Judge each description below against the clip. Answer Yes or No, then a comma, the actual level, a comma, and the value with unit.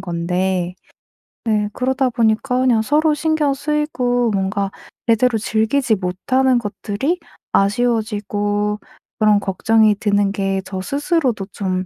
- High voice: Yes, high, 220 Hz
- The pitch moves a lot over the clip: No, average, 4.3 semitones